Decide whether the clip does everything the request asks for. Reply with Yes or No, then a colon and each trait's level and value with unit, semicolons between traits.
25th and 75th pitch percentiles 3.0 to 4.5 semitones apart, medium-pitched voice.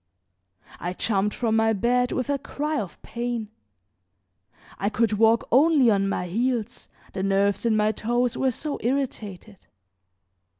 No: average, 3.3 semitones; high, 225 Hz